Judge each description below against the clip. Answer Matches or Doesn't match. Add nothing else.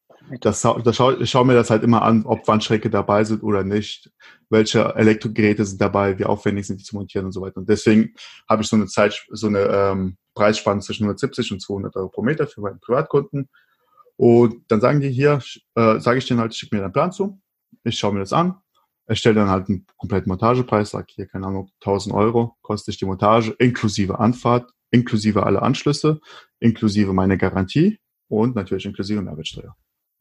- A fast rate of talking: Matches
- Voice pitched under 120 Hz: Matches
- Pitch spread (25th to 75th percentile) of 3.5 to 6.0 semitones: Doesn't match